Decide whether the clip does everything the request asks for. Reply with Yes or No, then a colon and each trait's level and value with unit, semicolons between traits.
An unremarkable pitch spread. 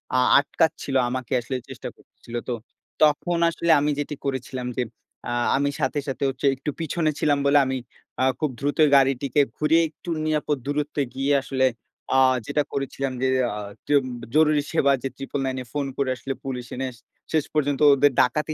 No: narrow, 2.1 semitones